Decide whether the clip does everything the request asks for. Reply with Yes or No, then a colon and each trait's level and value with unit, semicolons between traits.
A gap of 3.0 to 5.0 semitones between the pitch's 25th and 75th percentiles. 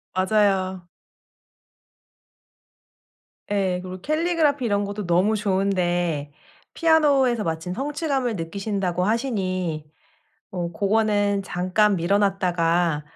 Yes: average, 3.6 semitones